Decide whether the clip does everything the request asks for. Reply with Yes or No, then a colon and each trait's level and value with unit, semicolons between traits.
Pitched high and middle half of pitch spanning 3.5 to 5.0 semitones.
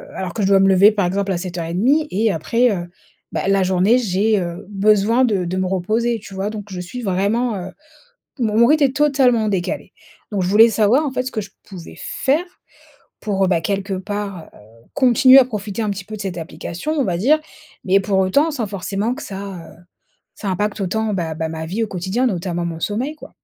Yes: high, 200 Hz; average, 3.8 semitones